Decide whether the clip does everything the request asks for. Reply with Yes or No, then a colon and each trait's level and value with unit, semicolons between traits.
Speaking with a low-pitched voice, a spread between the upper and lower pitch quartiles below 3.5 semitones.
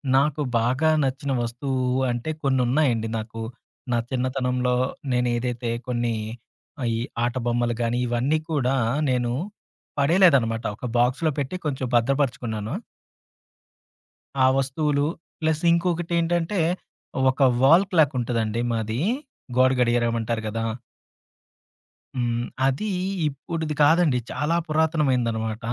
No: low, 130 Hz; average, 4.1 semitones